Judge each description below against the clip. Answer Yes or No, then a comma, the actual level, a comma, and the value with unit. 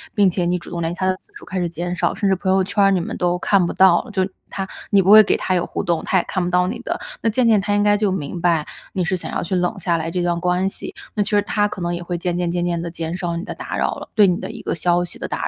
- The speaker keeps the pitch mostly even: Yes, narrow, 2.2 semitones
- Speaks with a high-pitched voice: No, medium, 180 Hz